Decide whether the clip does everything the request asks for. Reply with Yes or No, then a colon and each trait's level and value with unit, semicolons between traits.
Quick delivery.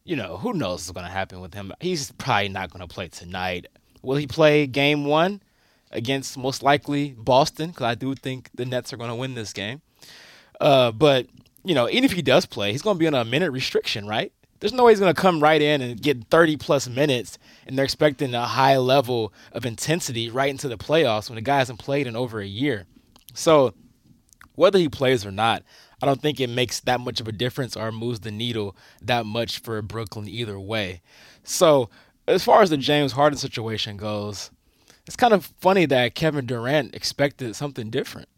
Yes: fast, 210 wpm